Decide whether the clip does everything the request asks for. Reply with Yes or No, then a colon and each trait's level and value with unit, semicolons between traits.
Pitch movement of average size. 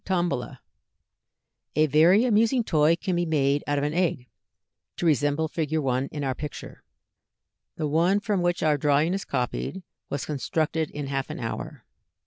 Yes: average, 3.5 semitones